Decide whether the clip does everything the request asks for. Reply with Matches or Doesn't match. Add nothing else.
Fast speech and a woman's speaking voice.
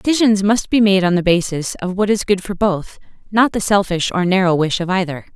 Matches